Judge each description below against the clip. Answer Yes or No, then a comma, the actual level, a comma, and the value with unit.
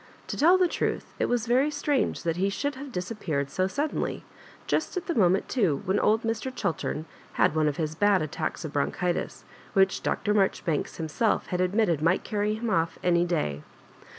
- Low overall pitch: No, high, 190 Hz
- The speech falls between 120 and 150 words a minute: No, average, 190 wpm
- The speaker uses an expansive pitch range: Yes, wide, 5.7 semitones